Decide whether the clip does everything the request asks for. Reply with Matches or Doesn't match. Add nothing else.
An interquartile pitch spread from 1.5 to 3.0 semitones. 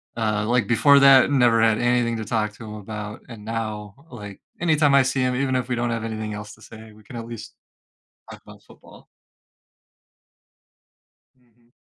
Matches